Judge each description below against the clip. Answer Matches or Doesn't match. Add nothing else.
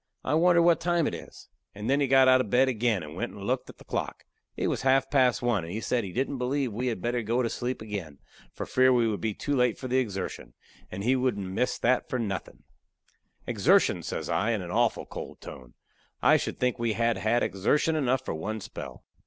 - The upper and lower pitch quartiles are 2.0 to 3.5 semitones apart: Doesn't match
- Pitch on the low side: Matches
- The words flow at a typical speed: Doesn't match